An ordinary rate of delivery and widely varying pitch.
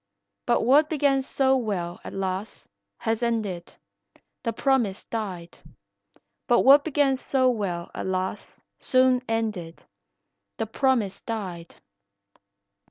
No: slow, 100 wpm; wide, 5.7 semitones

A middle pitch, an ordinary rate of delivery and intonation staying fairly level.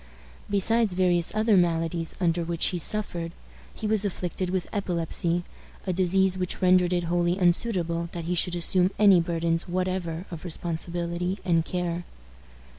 Yes: medium, 175 Hz; average, 145 wpm; narrow, 1.7 semitones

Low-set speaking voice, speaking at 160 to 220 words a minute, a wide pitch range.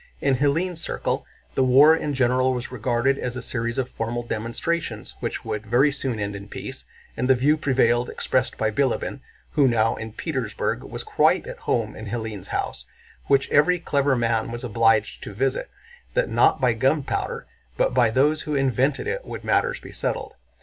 No: low, 130 Hz; average, 175 wpm; average, 3.9 semitones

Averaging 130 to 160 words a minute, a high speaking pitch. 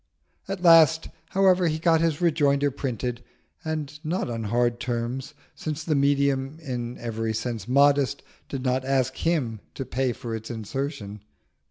No: average, 150 wpm; low, 135 Hz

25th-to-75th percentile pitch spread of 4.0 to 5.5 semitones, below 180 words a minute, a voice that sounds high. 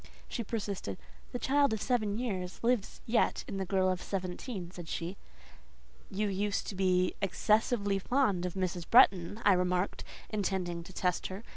No: average, 2.9 semitones; average, 160 wpm; high, 195 Hz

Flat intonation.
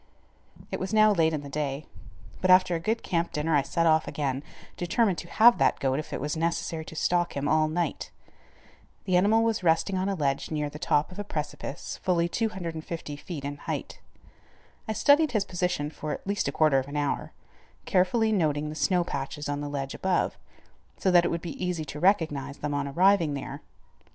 No: average, 4.0 semitones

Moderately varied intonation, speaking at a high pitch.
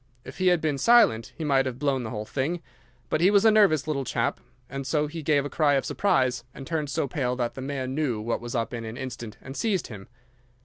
No: average, 4.0 semitones; medium, 140 Hz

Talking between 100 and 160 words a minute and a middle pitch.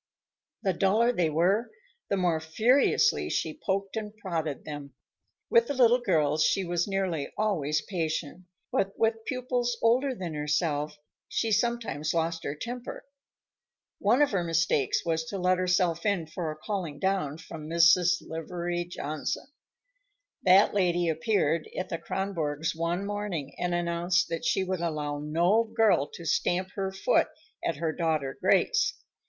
Yes: average, 150 wpm; medium, 175 Hz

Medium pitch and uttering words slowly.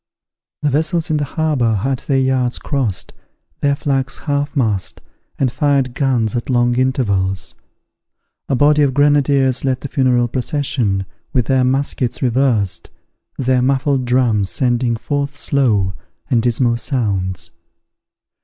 No: low, 130 Hz; slow, 130 wpm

